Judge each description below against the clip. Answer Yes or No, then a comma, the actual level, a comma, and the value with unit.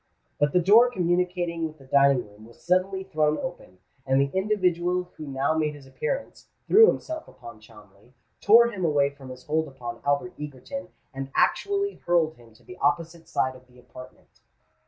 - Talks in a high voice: No, medium, 155 Hz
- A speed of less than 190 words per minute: Yes, average, 175 wpm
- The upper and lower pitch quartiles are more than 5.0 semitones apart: Yes, wide, 5.5 semitones